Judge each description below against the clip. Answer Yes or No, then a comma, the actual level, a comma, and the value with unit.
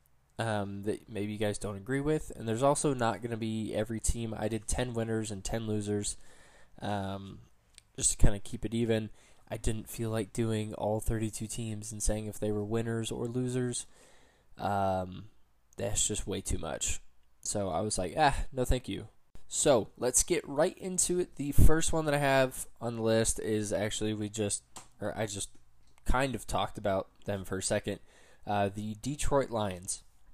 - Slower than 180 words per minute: No, average, 190 wpm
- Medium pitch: No, low, 110 Hz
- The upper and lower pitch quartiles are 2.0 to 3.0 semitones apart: Yes, narrow, 2.4 semitones